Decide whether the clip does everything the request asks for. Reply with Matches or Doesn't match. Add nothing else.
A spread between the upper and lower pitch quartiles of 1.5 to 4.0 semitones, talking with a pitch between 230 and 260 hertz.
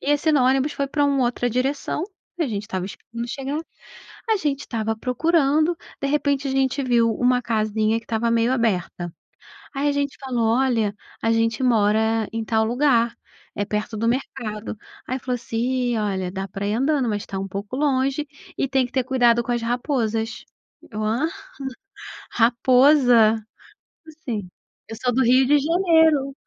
Matches